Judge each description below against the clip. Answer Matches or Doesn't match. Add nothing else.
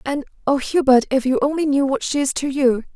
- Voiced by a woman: Matches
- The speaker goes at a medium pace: Doesn't match